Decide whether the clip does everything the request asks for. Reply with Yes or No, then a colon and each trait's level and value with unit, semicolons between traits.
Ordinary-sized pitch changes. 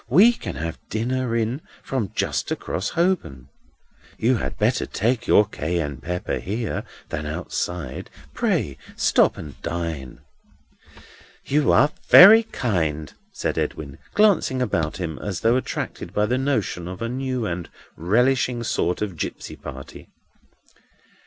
No: wide, 7.8 semitones